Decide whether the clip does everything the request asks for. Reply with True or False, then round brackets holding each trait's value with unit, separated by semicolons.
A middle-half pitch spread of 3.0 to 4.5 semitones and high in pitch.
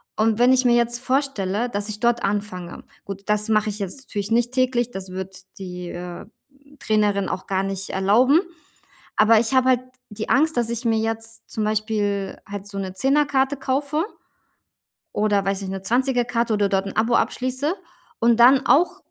True (3.9 semitones; 220 Hz)